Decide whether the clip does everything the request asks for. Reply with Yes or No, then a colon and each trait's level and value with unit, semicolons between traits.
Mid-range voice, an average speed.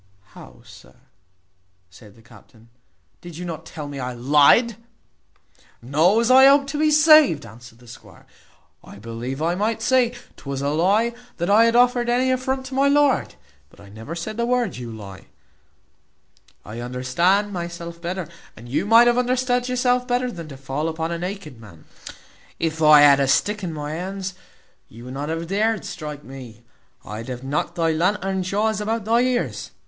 Yes: medium, 170 Hz; average, 180 wpm